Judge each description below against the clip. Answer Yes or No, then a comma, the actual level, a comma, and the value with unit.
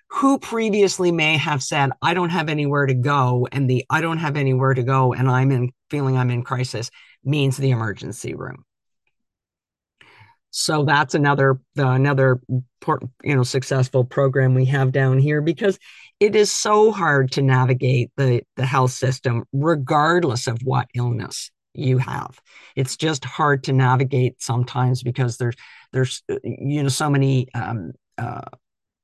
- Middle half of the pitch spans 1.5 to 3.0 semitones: Yes, average, 2.7 semitones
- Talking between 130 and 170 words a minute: Yes, average, 155 wpm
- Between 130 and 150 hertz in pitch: Yes, low, 135 Hz